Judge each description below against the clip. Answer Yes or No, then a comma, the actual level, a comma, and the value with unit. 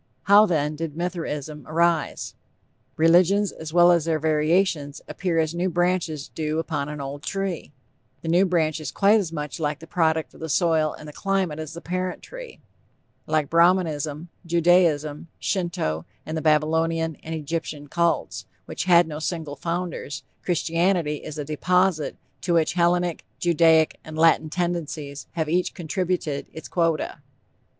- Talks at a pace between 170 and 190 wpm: No, average, 150 wpm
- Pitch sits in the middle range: Yes, medium, 165 Hz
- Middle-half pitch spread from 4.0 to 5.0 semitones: No, narrow, 2.4 semitones